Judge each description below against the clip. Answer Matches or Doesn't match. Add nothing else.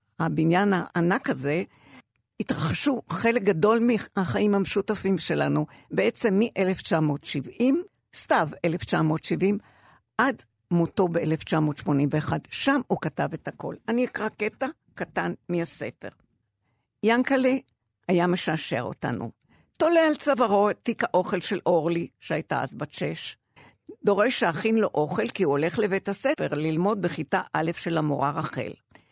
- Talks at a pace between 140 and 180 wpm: Doesn't match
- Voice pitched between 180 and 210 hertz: Matches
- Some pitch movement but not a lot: Doesn't match